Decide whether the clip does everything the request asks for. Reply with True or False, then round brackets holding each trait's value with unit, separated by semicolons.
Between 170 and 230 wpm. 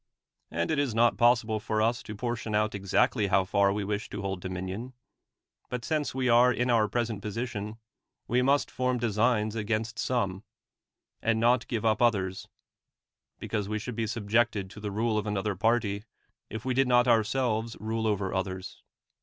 True (175 wpm)